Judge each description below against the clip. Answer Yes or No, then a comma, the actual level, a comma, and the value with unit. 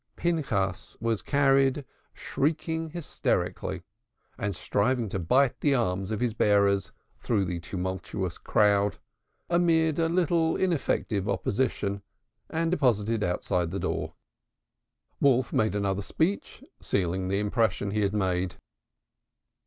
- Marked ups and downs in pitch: Yes, wide, 6.6 semitones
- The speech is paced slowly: Yes, slow, 115 wpm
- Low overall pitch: Yes, low, 110 Hz